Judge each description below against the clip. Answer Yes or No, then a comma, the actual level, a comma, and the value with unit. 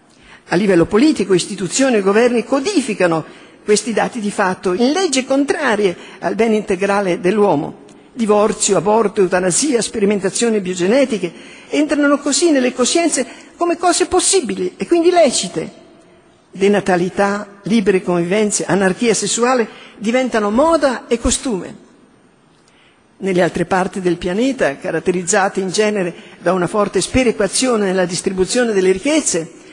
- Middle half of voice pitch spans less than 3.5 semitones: No, wide, 5.4 semitones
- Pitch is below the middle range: No, high, 210 Hz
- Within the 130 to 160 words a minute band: No, slow, 115 wpm